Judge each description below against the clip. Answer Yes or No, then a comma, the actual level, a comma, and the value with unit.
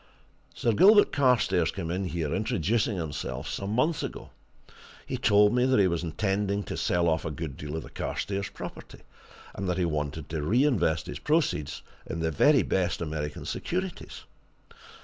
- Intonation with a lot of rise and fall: Yes, wide, 5.9 semitones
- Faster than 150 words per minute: Yes, average, 170 wpm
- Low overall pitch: Yes, very low, 95 Hz